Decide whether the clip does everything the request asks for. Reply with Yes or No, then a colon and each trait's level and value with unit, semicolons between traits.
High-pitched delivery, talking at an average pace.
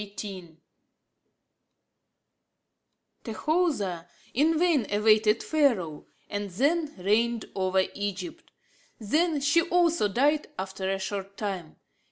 No: high, 210 Hz; slow, 95 wpm